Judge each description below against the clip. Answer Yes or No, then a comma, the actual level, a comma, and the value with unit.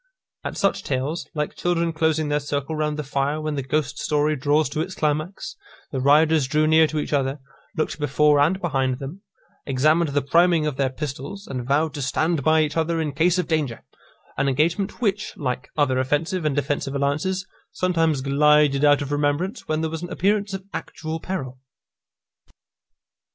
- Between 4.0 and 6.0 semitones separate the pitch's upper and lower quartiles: No, narrow, 2.5 semitones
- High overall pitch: No, medium, 150 Hz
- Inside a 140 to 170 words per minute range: No, average, 180 wpm